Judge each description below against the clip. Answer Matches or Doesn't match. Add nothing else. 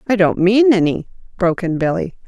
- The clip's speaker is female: Matches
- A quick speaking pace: Doesn't match